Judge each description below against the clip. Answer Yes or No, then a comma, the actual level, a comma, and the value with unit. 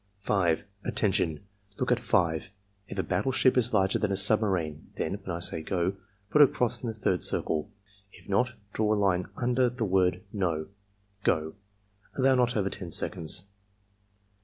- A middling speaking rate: Yes, average, 170 wpm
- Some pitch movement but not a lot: Yes, average, 4.0 semitones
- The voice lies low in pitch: Yes, low, 100 Hz